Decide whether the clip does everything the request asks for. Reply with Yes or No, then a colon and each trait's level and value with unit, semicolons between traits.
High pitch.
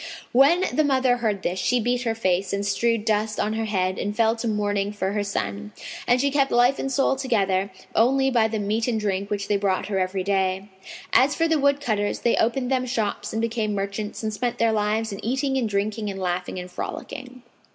Yes: high, 215 Hz